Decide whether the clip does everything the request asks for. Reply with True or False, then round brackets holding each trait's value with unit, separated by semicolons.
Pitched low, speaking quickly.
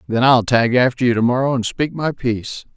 True (125 Hz; 215 wpm)